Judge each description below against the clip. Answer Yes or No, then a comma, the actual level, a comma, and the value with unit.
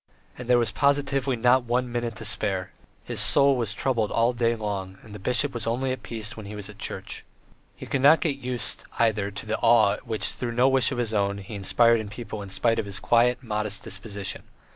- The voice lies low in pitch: Yes, low, 115 Hz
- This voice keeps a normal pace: No, fast, 225 wpm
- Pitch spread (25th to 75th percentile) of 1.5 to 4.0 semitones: Yes, average, 3.0 semitones